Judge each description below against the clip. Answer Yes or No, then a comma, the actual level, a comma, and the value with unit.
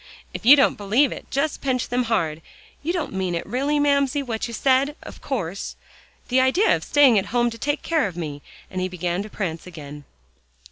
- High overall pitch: Yes, high, 235 Hz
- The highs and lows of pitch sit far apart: Yes, wide, 7.2 semitones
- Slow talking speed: No, fast, 205 wpm